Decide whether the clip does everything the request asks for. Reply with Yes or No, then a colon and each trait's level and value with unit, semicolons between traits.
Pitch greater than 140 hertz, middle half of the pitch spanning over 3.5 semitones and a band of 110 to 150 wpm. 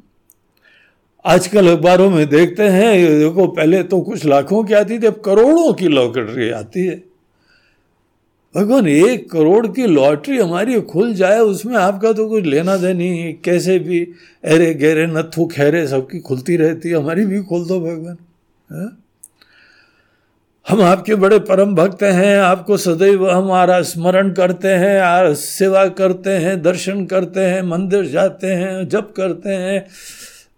No: medium, 185 Hz; narrow, 2.5 semitones; average, 145 wpm